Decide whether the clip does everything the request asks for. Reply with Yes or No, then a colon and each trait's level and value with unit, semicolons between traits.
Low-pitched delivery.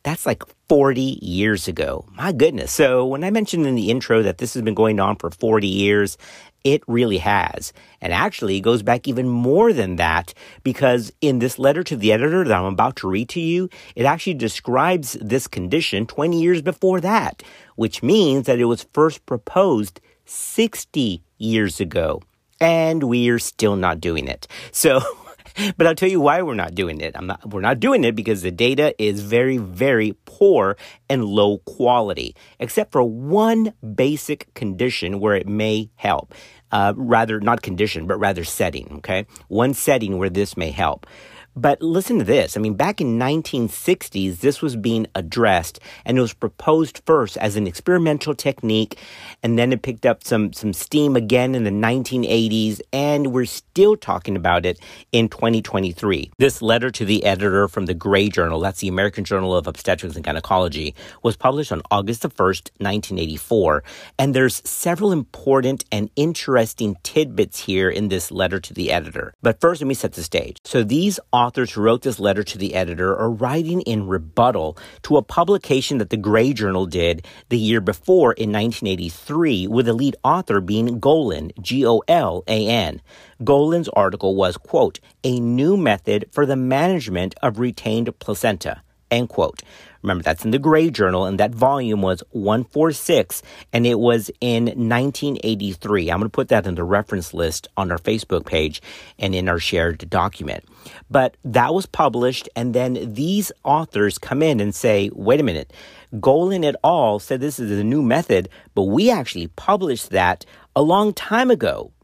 Yes: low, 115 Hz